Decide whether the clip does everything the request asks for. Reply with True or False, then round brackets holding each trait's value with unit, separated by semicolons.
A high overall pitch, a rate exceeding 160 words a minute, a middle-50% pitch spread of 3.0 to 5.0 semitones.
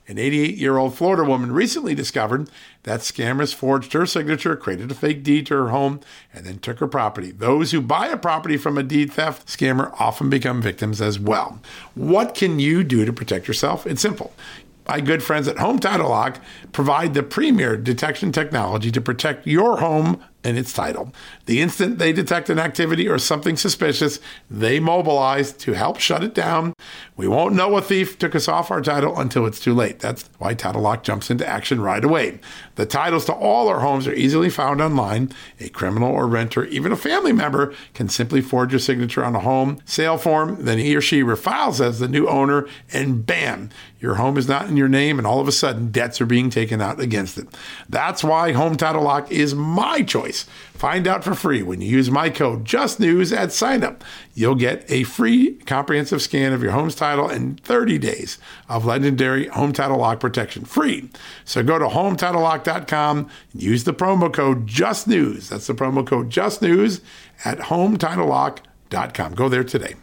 False (140 Hz; 190 wpm; 4.1 semitones)